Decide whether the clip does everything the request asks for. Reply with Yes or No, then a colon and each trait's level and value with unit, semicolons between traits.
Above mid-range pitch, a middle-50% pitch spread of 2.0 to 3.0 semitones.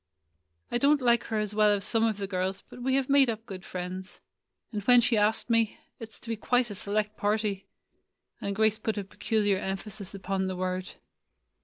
Yes: high, 210 Hz; average, 2.7 semitones